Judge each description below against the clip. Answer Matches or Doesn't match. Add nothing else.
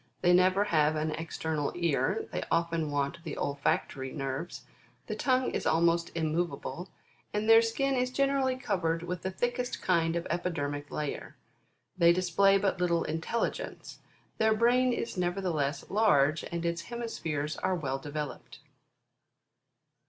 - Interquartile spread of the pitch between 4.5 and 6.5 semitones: Matches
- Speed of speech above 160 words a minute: Doesn't match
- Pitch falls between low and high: Matches